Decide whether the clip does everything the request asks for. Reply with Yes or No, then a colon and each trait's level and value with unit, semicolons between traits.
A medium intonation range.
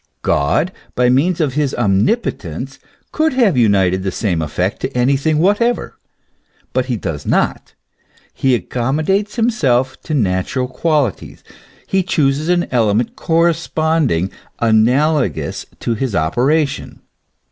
No: wide, 6.6 semitones